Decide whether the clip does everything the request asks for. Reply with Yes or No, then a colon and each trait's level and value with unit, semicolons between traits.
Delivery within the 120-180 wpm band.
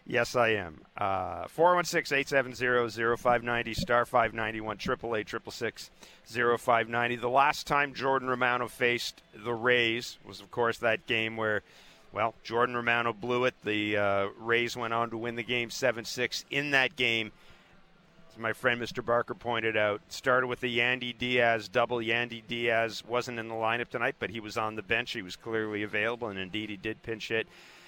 Yes: average, 165 wpm